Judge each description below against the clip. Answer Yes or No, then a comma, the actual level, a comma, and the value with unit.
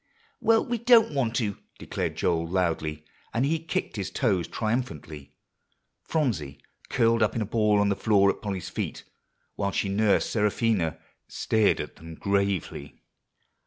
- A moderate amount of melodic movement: Yes, average, 5.0 semitones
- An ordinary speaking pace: Yes, average, 150 wpm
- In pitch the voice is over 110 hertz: No, low, 100 Hz